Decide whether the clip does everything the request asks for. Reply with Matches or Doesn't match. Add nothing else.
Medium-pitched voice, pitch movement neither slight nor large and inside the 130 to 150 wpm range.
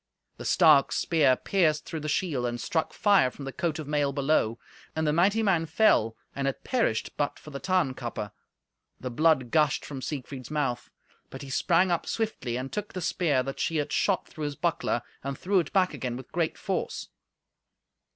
Doesn't match